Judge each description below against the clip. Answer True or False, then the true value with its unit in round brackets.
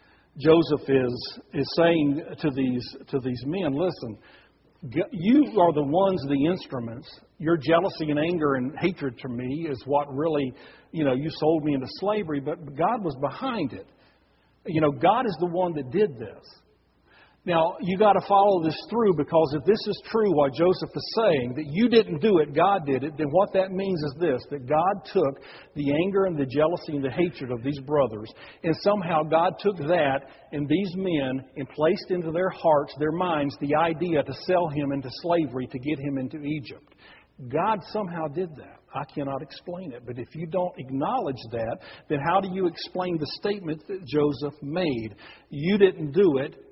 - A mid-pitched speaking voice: True (155 Hz)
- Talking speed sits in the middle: True (190 wpm)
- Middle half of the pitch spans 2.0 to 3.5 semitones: False (4.5 semitones)